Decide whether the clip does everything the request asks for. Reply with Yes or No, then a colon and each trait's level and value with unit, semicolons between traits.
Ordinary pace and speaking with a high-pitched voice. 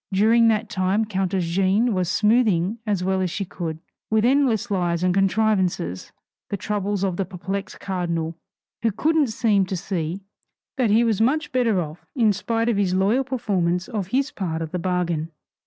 Yes: average, 175 wpm; high, 195 Hz